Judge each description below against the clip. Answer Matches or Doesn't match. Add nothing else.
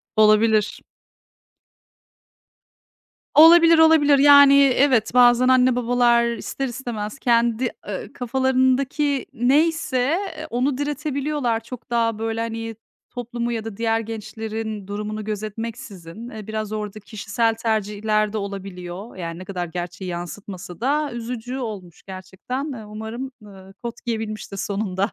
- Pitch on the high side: Matches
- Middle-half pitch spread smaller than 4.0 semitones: Matches